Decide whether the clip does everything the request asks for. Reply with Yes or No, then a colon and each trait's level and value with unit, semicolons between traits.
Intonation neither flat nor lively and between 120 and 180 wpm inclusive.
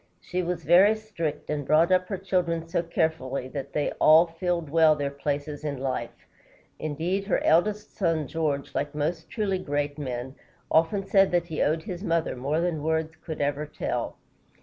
Yes: average, 3.3 semitones; average, 175 wpm